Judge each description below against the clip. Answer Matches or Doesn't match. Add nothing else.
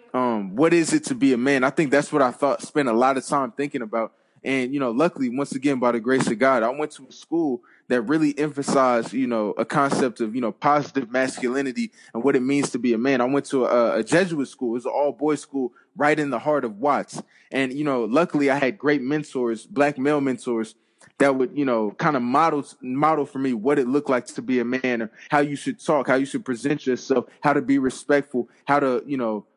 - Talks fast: Matches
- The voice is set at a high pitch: Doesn't match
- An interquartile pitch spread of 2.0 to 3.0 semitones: Matches